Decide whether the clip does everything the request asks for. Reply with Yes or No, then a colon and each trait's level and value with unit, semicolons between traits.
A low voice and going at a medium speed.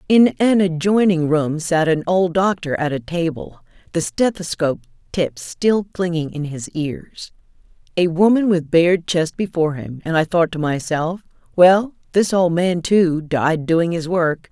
No: medium, 170 Hz; average, 165 wpm